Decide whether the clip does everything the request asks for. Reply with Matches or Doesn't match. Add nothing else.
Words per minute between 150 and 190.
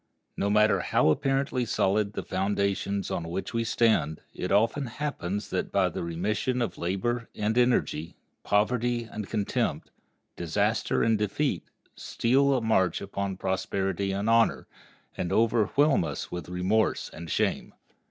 Doesn't match